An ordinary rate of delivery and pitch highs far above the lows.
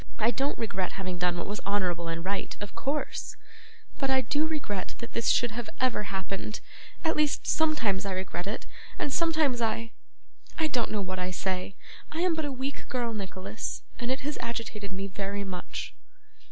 Yes: average, 185 wpm; wide, 5.8 semitones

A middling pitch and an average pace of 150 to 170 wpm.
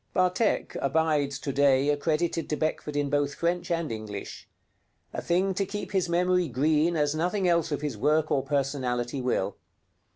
Yes: medium, 150 Hz; average, 165 wpm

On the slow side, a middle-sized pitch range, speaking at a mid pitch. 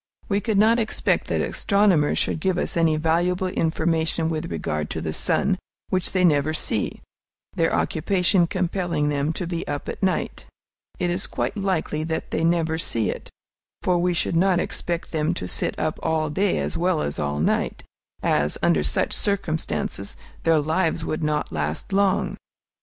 No: average, 170 wpm; average, 3.2 semitones; medium, 165 Hz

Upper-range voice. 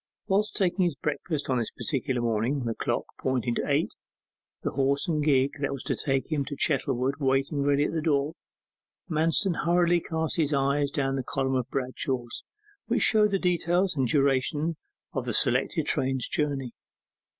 No: medium, 140 Hz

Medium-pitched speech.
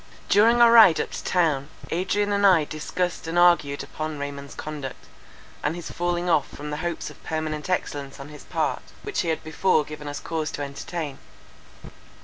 Yes: medium, 160 Hz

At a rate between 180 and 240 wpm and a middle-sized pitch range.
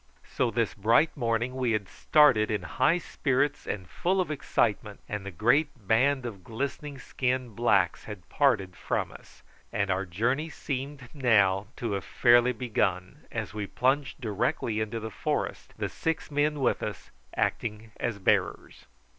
No: average, 155 wpm; average, 4.7 semitones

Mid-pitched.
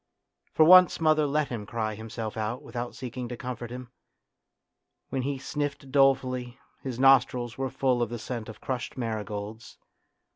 No: low, 125 Hz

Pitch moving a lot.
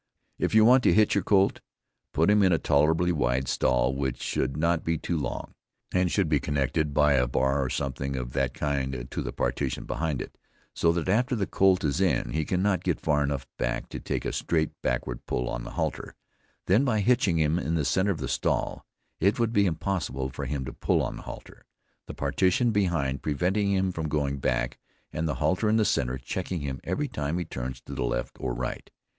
Yes: wide, 5.7 semitones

